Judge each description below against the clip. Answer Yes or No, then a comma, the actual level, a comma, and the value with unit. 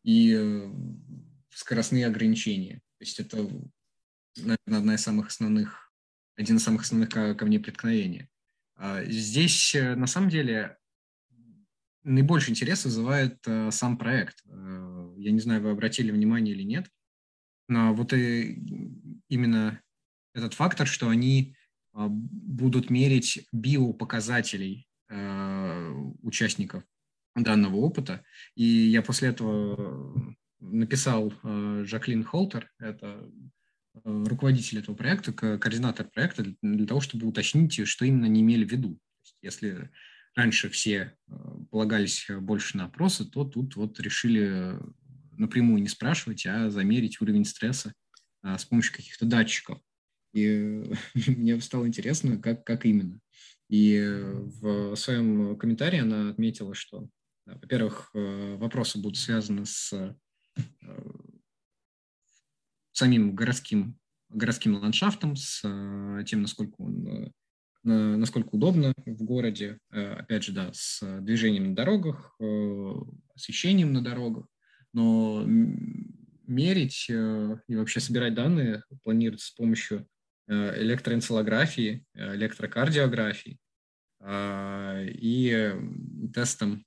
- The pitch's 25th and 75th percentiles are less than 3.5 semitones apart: No, average, 4.4 semitones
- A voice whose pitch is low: Yes, low, 115 Hz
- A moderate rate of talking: No, slow, 100 wpm